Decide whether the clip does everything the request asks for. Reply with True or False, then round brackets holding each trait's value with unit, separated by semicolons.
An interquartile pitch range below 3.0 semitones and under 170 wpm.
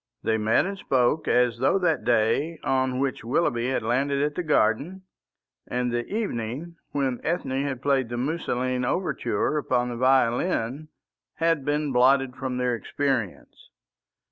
False (3.4 semitones; 145 wpm)